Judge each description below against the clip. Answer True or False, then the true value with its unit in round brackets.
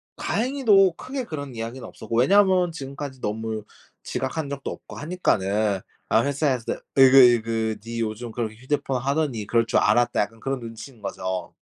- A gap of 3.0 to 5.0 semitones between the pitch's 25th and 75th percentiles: True (4.3 semitones)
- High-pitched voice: False (125 Hz)